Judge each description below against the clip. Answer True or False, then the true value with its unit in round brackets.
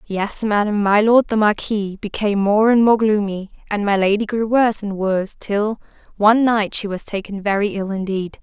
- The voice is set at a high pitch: True (205 Hz)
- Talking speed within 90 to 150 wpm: False (190 wpm)